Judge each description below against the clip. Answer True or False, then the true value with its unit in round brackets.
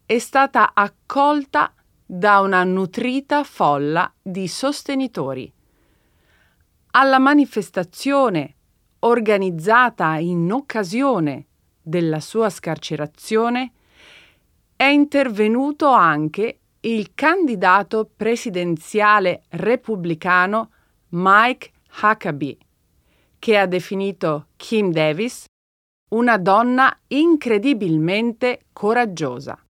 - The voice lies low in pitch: False (205 Hz)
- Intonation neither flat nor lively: False (6.9 semitones)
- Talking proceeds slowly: True (70 wpm)